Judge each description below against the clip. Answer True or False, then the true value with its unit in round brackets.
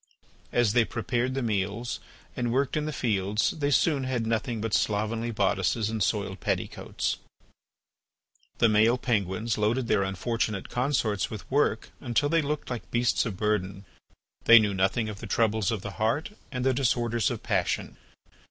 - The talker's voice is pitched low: True (115 Hz)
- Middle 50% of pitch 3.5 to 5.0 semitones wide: False (2.9 semitones)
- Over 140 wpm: True (160 wpm)